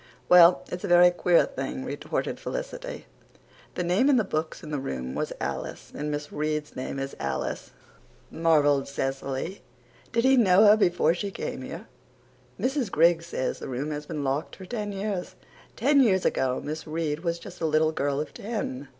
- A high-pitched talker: No, medium, 165 Hz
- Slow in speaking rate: No, average, 180 wpm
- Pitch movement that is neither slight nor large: Yes, average, 5.0 semitones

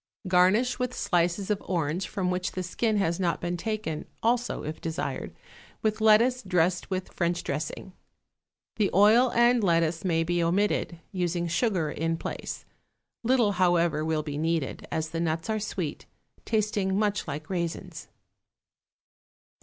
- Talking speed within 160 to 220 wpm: No, average, 145 wpm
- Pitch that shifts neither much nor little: Yes, average, 4.3 semitones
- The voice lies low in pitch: No, medium, 180 Hz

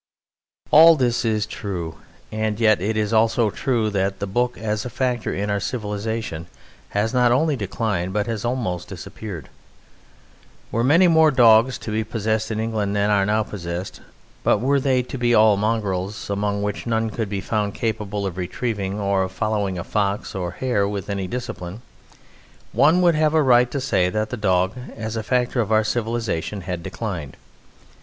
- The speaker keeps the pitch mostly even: No, average, 3.1 semitones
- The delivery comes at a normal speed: Yes, average, 180 wpm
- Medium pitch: No, low, 110 Hz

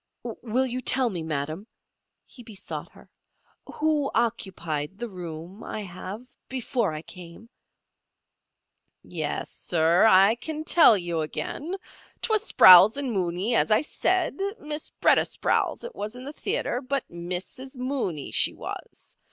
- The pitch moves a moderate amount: No, wide, 7.0 semitones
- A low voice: No, high, 220 Hz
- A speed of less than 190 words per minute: Yes, slow, 135 wpm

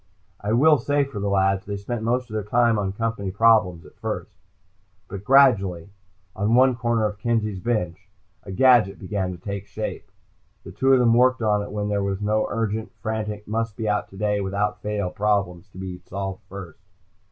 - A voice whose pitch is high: No, low, 105 Hz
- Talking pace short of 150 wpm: No, average, 190 wpm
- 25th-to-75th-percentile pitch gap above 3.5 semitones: No, average, 2.7 semitones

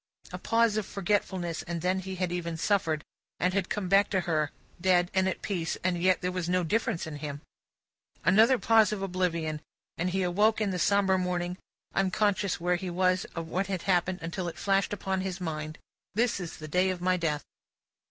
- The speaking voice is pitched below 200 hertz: Yes, medium, 185 Hz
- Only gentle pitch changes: Yes, narrow, 2.2 semitones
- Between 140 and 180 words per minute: No, average, 200 wpm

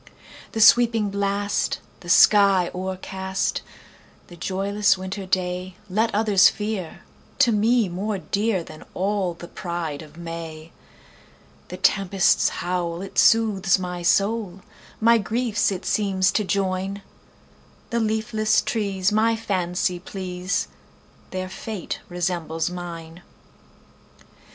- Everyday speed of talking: No, slow, 95 wpm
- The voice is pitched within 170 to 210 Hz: Yes, high, 190 Hz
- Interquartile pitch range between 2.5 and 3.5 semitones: Yes, average, 2.8 semitones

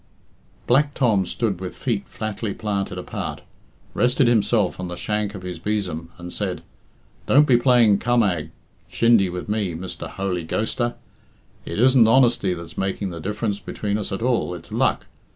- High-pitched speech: No, low, 105 Hz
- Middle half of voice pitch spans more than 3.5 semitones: Yes, average, 4.4 semitones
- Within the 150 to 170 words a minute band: Yes, average, 160 wpm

